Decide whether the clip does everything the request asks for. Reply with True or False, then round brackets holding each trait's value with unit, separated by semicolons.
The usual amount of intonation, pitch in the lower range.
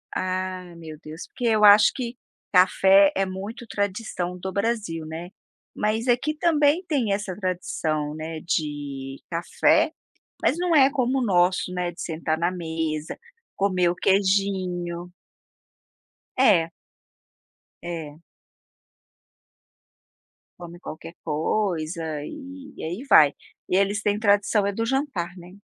False (4.2 semitones; 185 Hz)